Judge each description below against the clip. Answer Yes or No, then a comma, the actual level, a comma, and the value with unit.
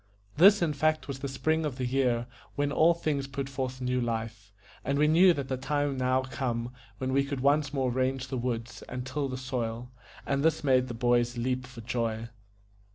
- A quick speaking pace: Yes, fast, 210 wpm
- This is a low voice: Yes, low, 130 Hz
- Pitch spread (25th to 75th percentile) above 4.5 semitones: No, narrow, 2.4 semitones